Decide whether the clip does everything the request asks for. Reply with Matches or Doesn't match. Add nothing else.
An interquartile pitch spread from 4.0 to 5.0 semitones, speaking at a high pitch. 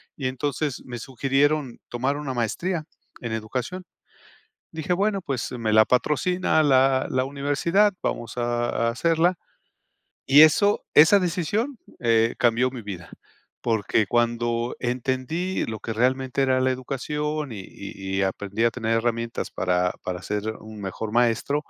Doesn't match